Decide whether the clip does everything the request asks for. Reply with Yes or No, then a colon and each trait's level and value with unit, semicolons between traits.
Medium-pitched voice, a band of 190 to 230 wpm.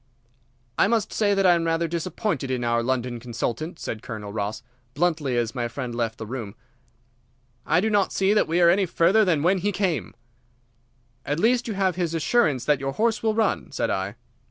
Yes: medium, 165 Hz; average, 200 wpm